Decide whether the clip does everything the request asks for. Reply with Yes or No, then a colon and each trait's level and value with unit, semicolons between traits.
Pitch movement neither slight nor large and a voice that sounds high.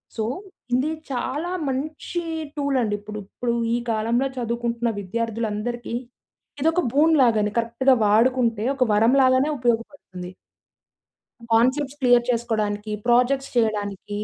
Yes: average, 3.2 semitones; high, 235 Hz